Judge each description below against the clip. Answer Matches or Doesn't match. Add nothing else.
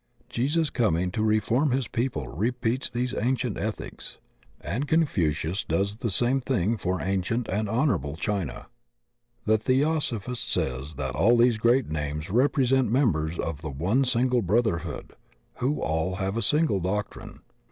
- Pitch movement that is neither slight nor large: Doesn't match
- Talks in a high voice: Doesn't match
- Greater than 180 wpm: Doesn't match